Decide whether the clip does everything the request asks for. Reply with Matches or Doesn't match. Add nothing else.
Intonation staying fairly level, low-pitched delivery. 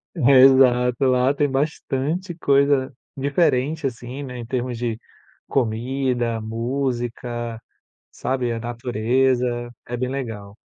Matches